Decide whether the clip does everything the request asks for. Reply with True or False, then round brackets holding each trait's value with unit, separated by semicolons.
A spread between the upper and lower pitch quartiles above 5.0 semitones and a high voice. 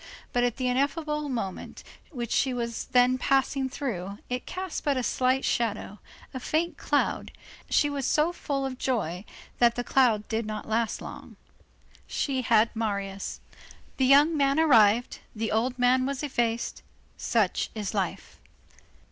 False (3.6 semitones; 250 Hz)